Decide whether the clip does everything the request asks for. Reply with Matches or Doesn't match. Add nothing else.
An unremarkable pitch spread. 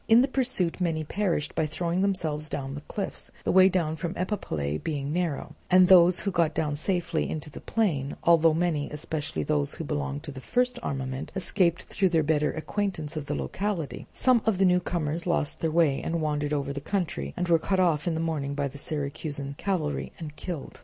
Matches